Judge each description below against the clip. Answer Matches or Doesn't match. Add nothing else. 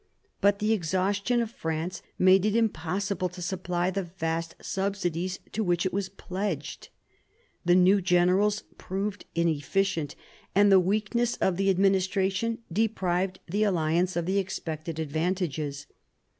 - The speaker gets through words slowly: Matches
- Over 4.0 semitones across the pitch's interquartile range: Doesn't match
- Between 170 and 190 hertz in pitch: Matches